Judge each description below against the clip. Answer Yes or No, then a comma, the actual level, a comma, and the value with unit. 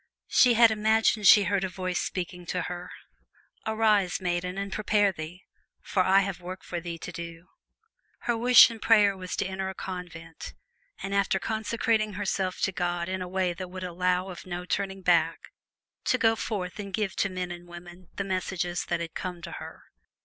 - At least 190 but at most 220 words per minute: Yes, average, 195 wpm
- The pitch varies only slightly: Yes, narrow, 2.2 semitones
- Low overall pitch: No, medium, 185 Hz